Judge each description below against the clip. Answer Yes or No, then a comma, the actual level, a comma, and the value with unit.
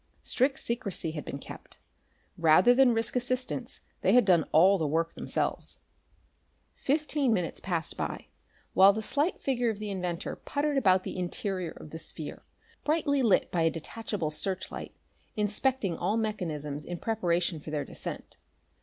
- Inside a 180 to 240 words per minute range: No, average, 155 wpm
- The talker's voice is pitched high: Yes, high, 195 Hz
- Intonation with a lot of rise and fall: Yes, wide, 6.6 semitones